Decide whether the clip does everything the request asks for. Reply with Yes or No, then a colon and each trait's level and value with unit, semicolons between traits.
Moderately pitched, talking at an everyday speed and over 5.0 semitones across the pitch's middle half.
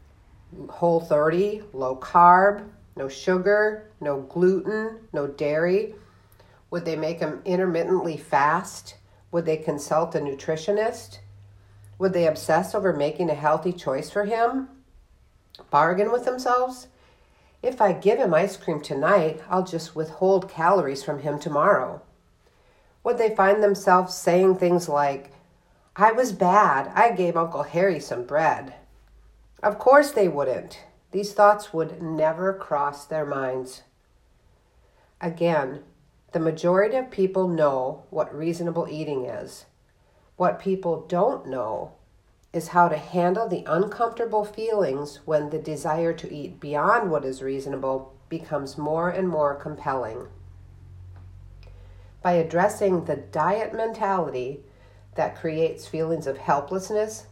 No: medium, 165 Hz; slow, 125 wpm; wide, 5.5 semitones